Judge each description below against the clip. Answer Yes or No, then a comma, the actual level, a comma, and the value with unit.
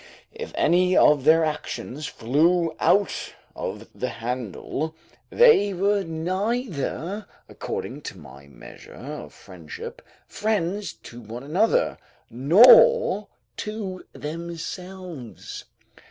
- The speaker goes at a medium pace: No, slow, 95 wpm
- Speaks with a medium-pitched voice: Yes, medium, 170 Hz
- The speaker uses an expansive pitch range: Yes, wide, 6.5 semitones